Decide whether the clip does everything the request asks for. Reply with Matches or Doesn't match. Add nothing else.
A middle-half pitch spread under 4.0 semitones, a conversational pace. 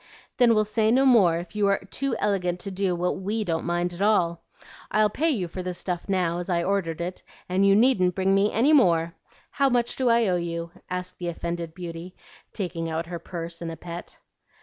Doesn't match